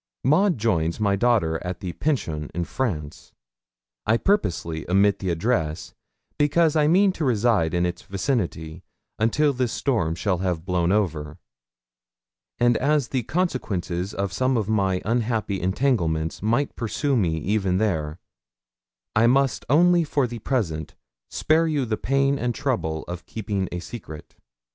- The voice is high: No, low, 105 Hz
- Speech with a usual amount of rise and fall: No, wide, 7.2 semitones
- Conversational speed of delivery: Yes, average, 145 wpm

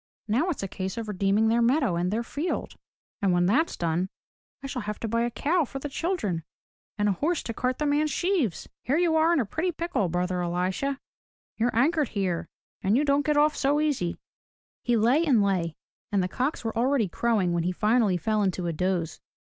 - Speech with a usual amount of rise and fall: No, wide, 7.5 semitones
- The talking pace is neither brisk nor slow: No, fast, 210 wpm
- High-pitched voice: Yes, high, 230 Hz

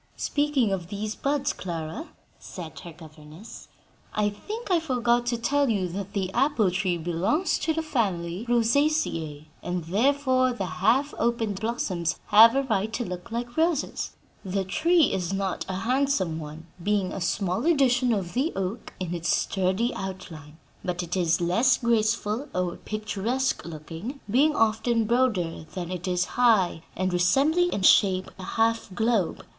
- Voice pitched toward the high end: Yes, high, 210 Hz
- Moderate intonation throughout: No, wide, 5.7 semitones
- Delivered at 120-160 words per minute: Yes, average, 155 wpm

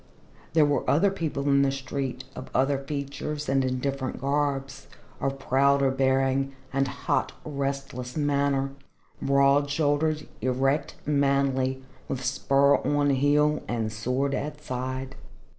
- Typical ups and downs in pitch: No, narrow, 1.4 semitones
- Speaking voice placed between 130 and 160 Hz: Yes, medium, 140 Hz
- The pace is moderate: No, slow, 125 wpm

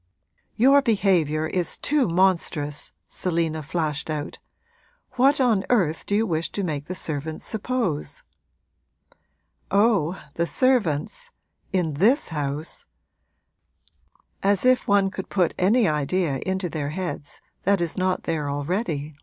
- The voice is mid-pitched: Yes, medium, 180 Hz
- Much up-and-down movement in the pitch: No, average, 4.8 semitones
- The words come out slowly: Yes, slow, 125 wpm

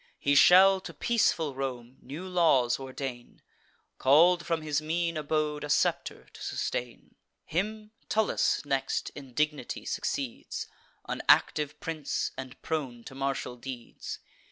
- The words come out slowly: Yes, slow, 130 wpm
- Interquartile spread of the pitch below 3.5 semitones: No, average, 3.8 semitones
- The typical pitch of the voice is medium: Yes, medium, 150 Hz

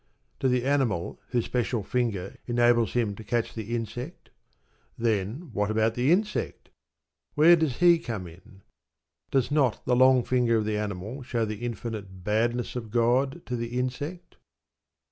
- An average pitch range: Yes, average, 3.0 semitones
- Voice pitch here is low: Yes, low, 120 Hz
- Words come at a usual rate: Yes, average, 155 wpm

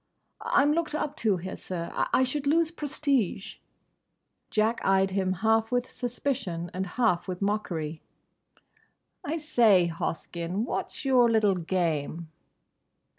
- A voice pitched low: No, high, 210 Hz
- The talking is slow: Yes, slow, 125 wpm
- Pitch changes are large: Yes, wide, 6.2 semitones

